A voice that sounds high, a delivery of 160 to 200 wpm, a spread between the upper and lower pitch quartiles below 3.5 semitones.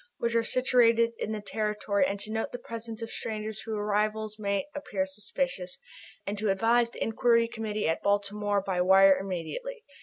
Yes: high, 215 Hz; average, 180 wpm; narrow, 2.4 semitones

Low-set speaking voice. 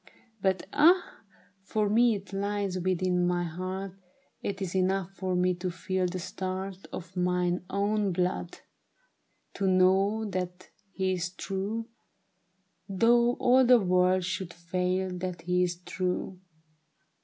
No: medium, 185 Hz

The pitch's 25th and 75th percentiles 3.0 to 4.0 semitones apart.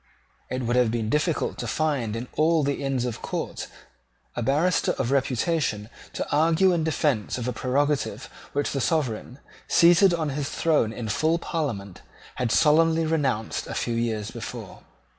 No: average, 5.1 semitones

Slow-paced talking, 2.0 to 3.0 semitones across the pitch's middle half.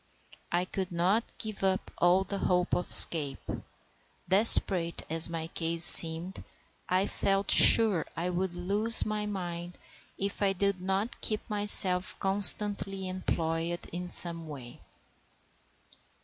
Yes: slow, 125 wpm; narrow, 2.6 semitones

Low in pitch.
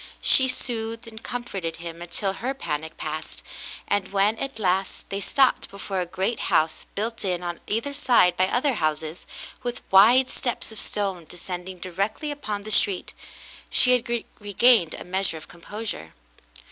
No: high, 200 Hz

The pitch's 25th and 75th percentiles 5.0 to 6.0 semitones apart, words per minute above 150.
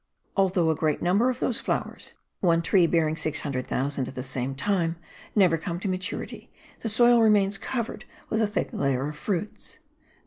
Yes: wide, 5.4 semitones; average, 170 wpm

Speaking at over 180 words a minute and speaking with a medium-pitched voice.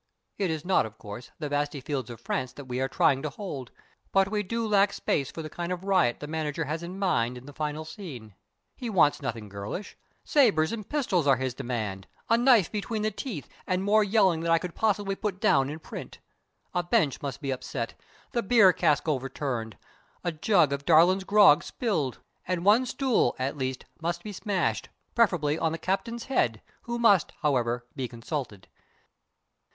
Yes: average, 190 wpm; medium, 160 Hz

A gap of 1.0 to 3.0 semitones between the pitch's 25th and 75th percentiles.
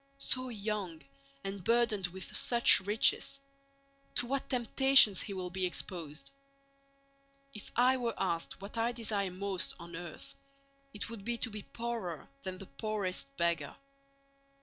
No: average, 4.4 semitones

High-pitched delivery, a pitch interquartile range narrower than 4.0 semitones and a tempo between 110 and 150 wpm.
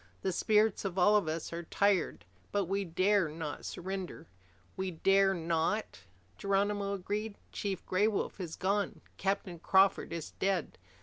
Yes: high, 195 Hz; average, 2.7 semitones; average, 145 wpm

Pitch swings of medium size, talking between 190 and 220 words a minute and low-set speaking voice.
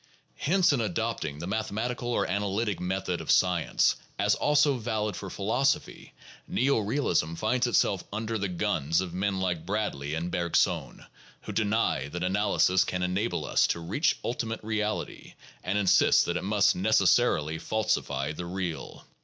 No: average, 4.0 semitones; average, 155 wpm; low, 100 Hz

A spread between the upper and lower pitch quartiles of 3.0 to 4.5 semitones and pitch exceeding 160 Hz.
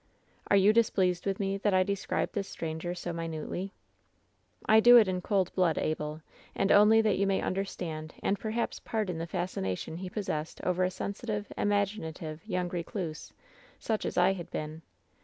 Yes: average, 3.5 semitones; medium, 185 Hz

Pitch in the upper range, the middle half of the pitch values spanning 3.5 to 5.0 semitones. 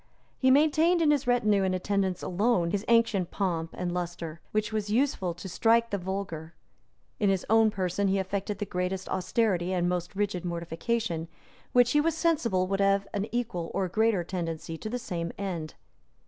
Yes: high, 195 Hz; average, 4.1 semitones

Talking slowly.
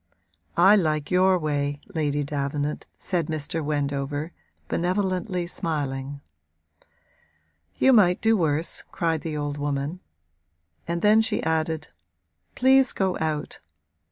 Yes: slow, 110 wpm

